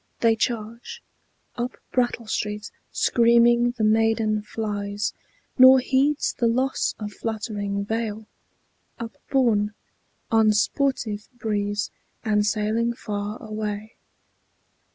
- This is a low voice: No, high, 220 Hz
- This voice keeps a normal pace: No, slow, 95 wpm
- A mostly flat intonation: Yes, narrow, 2.2 semitones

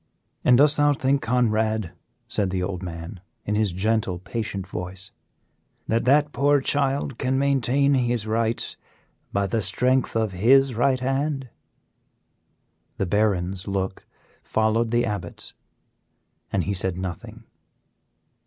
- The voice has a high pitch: No, low, 110 Hz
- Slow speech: Yes, slow, 125 wpm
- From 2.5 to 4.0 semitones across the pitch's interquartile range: No, wide, 5.4 semitones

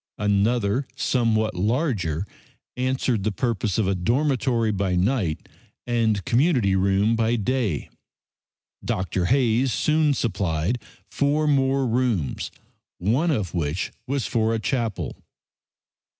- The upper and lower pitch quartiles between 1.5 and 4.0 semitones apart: No, average, 4.9 semitones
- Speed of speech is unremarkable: No, slow, 110 wpm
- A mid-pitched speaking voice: No, low, 115 Hz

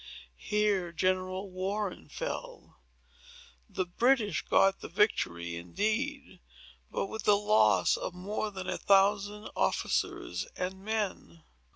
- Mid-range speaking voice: No, high, 195 Hz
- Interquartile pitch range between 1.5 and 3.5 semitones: Yes, average, 2.7 semitones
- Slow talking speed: Yes, slow, 110 wpm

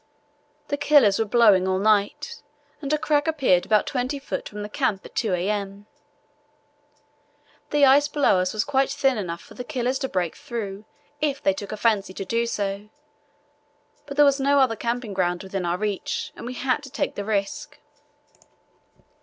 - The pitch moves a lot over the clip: Yes, wide, 5.7 semitones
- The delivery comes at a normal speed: Yes, average, 180 wpm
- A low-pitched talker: No, high, 225 Hz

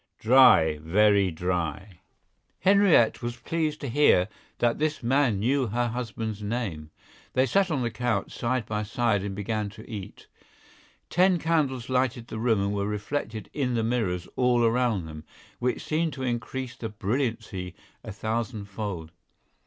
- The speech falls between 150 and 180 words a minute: Yes, average, 155 wpm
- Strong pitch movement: No, average, 4.1 semitones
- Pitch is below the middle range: Yes, low, 115 Hz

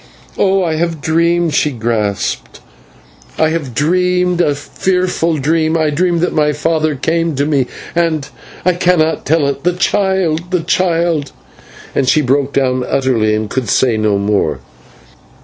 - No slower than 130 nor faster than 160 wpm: Yes, average, 155 wpm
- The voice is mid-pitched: Yes, medium, 155 Hz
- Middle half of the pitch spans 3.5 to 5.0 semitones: Yes, average, 4.3 semitones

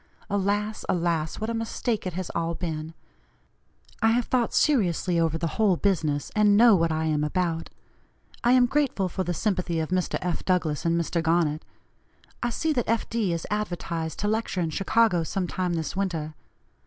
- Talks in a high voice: No, medium, 180 Hz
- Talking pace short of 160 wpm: No, average, 180 wpm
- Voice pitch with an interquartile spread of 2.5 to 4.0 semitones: No, average, 4.5 semitones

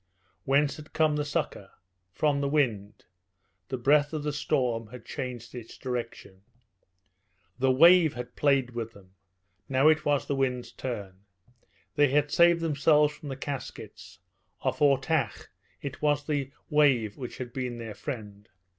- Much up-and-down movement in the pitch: No, average, 3.7 semitones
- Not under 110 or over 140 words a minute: No, average, 150 wpm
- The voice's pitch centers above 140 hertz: No, low, 135 Hz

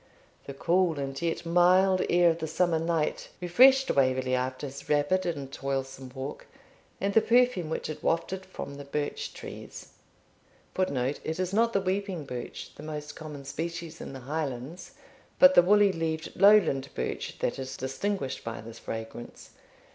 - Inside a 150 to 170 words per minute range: Yes, average, 160 wpm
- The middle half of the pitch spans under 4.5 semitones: No, average, 5.3 semitones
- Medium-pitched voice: Yes, medium, 160 Hz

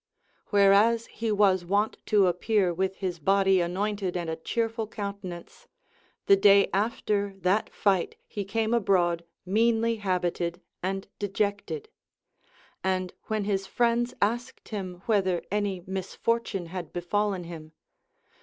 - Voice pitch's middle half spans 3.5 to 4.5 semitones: No, average, 2.7 semitones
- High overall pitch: Yes, high, 195 Hz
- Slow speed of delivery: Yes, slow, 125 wpm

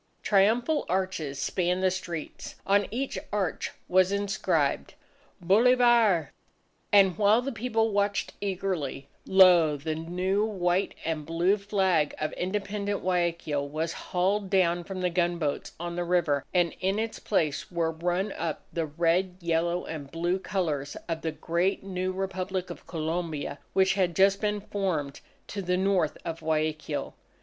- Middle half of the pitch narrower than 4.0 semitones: Yes, average, 3.1 semitones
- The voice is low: No, medium, 180 Hz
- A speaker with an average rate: Yes, average, 145 wpm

